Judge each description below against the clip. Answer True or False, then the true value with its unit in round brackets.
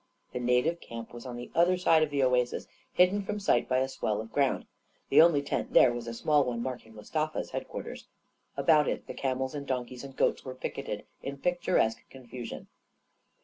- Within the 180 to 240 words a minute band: True (190 wpm)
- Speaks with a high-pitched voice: False (130 Hz)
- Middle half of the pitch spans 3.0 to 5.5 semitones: True (4.2 semitones)